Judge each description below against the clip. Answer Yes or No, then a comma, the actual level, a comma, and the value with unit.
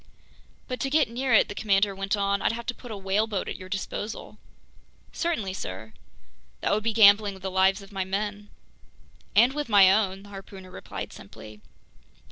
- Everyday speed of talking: Yes, average, 185 wpm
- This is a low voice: No, high, 200 Hz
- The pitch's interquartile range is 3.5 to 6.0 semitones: No, narrow, 2.4 semitones